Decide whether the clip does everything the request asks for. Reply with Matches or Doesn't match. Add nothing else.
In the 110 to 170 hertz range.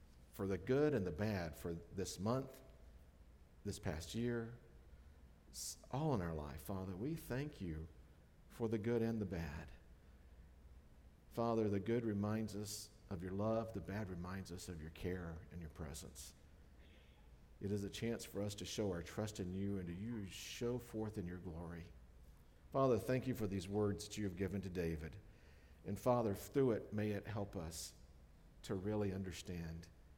Doesn't match